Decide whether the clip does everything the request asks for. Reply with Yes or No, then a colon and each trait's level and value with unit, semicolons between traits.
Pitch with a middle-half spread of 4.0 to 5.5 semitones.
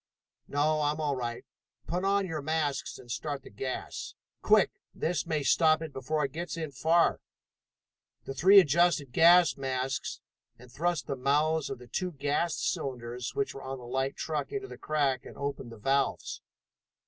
No: average, 3.5 semitones